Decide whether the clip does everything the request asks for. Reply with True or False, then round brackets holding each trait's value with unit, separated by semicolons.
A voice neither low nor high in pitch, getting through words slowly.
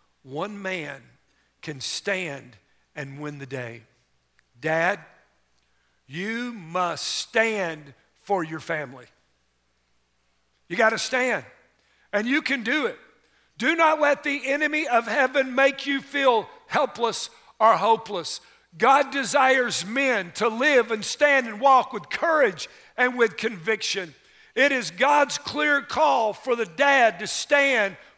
False (225 Hz; 130 wpm)